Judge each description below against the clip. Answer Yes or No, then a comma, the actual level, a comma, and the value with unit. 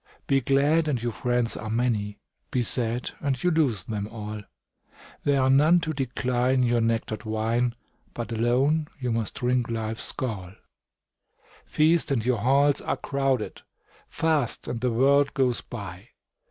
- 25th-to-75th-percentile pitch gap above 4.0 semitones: No, average, 3.4 semitones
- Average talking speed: Yes, average, 150 wpm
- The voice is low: Yes, low, 125 Hz